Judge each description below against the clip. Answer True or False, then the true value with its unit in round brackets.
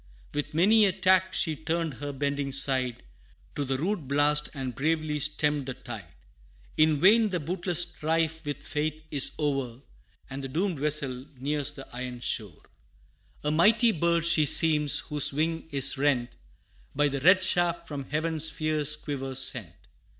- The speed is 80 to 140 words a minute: False (160 wpm)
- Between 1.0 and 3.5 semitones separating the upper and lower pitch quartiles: True (3.2 semitones)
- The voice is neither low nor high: True (150 Hz)